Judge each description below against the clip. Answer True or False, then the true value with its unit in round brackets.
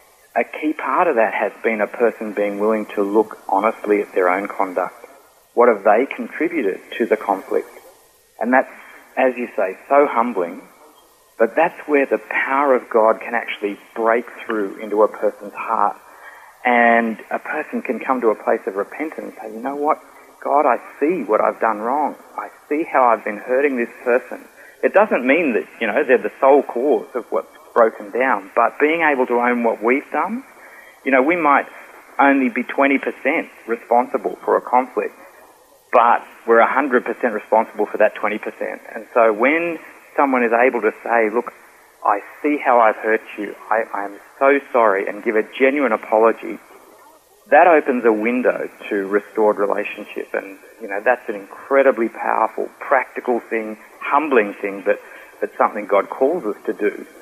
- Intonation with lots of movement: True (6.8 semitones)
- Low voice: True (130 Hz)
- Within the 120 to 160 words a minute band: False (175 wpm)